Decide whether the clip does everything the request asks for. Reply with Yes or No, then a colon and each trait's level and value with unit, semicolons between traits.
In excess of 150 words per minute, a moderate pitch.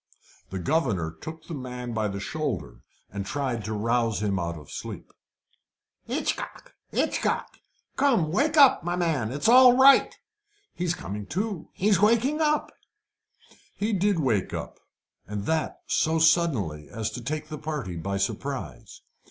No: average, 145 wpm; medium, 145 Hz